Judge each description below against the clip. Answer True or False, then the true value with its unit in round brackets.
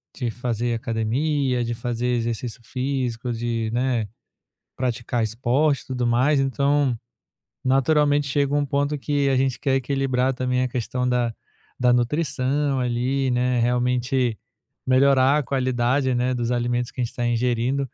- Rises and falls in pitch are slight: True (2.2 semitones)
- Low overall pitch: True (125 Hz)